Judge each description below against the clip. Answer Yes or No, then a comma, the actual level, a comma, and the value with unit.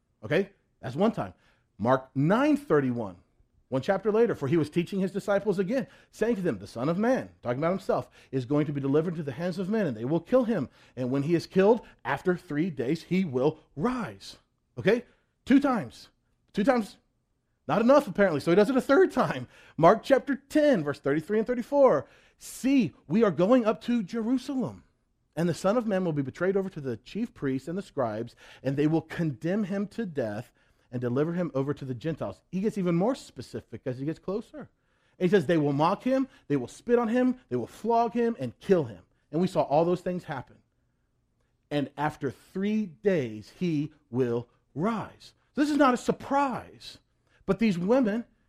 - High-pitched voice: No, medium, 175 Hz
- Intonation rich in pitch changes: Yes, wide, 8.4 semitones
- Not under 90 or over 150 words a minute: No, average, 200 wpm